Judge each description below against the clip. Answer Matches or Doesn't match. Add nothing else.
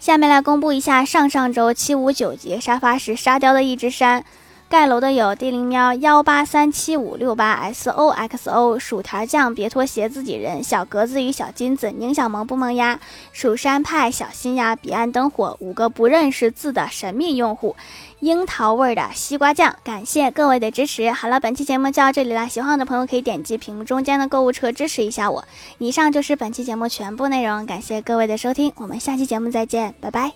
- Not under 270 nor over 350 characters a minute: Matches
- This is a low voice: Doesn't match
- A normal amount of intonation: Matches